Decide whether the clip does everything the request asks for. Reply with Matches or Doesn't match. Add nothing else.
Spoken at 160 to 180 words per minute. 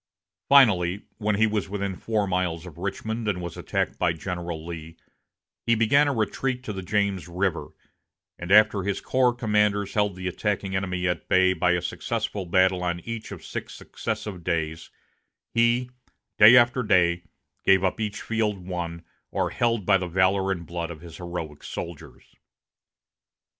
Matches